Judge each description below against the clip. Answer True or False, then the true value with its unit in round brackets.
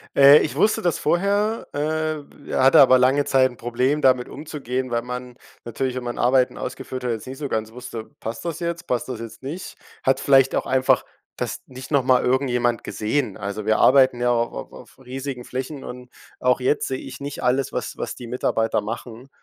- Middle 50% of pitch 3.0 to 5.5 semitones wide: False (2.4 semitones)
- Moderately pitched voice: False (130 Hz)